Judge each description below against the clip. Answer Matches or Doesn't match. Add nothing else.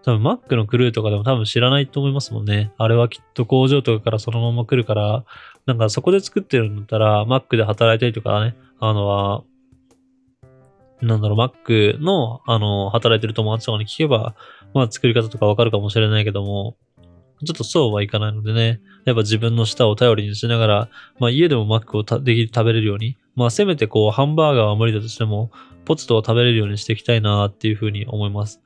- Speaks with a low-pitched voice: Matches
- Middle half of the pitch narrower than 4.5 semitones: Matches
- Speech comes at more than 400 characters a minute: Matches